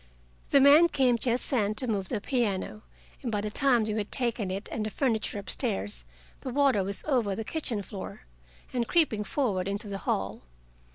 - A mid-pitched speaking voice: No, high, 220 Hz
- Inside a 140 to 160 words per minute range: No, average, 190 wpm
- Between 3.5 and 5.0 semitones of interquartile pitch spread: Yes, average, 4.2 semitones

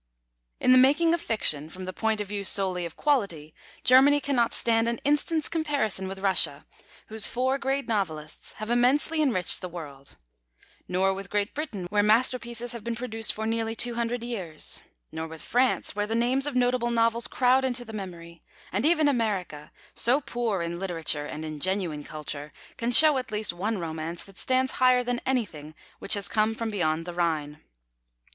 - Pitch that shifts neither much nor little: No, wide, 5.8 semitones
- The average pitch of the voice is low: No, high, 220 Hz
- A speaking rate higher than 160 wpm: Yes, average, 180 wpm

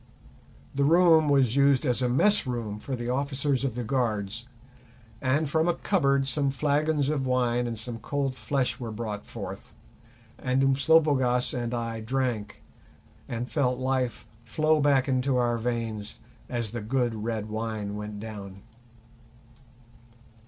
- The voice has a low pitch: Yes, low, 125 Hz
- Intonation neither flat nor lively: Yes, average, 3.4 semitones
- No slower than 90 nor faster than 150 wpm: Yes, average, 145 wpm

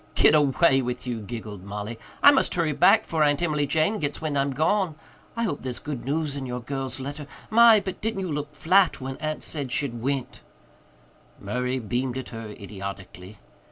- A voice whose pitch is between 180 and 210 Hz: No, medium, 140 Hz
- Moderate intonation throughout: Yes, average, 4.4 semitones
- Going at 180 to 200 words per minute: Yes, average, 190 wpm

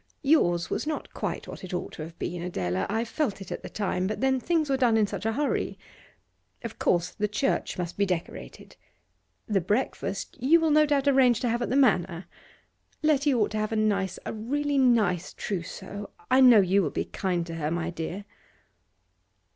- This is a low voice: No, high, 215 Hz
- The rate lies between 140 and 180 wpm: No, average, 200 wpm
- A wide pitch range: Yes, wide, 6.6 semitones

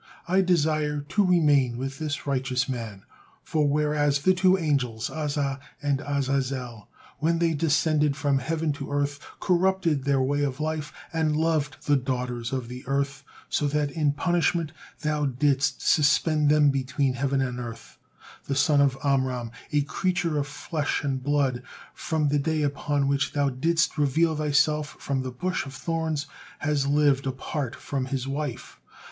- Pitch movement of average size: No, narrow, 2.2 semitones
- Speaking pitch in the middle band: Yes, medium, 145 Hz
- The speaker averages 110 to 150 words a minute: No, average, 160 wpm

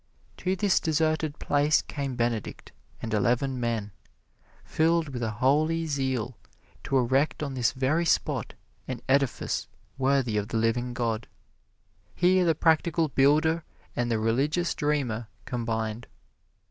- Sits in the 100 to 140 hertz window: Yes, low, 135 Hz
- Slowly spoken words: Yes, slow, 130 wpm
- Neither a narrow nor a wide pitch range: Yes, average, 4.8 semitones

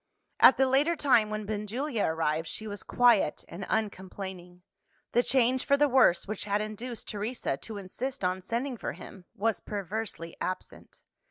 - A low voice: No, high, 215 Hz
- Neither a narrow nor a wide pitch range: Yes, average, 4.5 semitones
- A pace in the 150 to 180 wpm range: Yes, average, 160 wpm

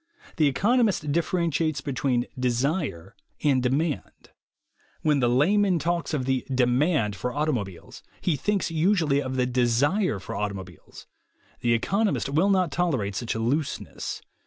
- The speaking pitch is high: No, medium, 140 Hz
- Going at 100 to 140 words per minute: Yes, slow, 135 wpm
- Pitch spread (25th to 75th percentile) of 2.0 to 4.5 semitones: No, wide, 5.6 semitones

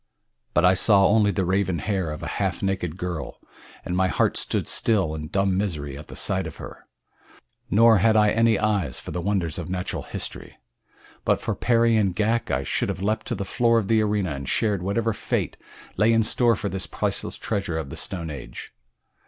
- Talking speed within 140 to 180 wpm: No, fast, 205 wpm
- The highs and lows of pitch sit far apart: No, average, 3.8 semitones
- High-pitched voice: No, very low, 95 Hz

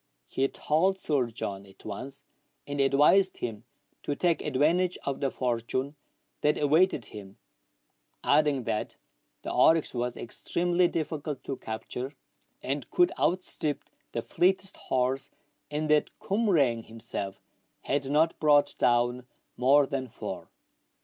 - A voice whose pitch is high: No, medium, 140 Hz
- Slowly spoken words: Yes, slow, 125 wpm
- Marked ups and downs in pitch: No, average, 4.2 semitones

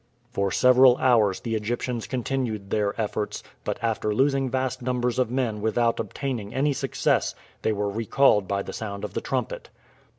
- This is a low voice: Yes, low, 115 Hz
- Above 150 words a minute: Yes, average, 165 wpm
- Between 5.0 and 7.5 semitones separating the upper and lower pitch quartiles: No, average, 3.5 semitones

